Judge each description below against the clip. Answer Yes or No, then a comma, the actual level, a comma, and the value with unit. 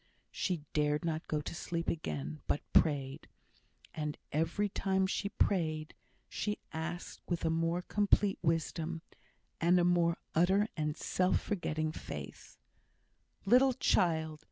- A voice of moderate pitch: Yes, medium, 165 Hz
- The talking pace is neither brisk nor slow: No, slow, 130 wpm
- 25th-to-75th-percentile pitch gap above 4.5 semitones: No, average, 3.0 semitones